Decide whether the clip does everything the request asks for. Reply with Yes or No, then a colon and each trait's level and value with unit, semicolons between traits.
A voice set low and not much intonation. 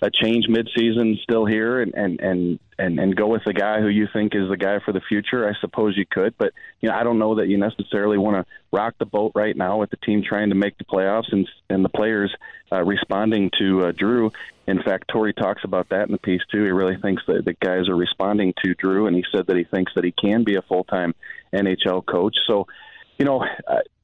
Yes: low, 105 Hz; narrow, 2.3 semitones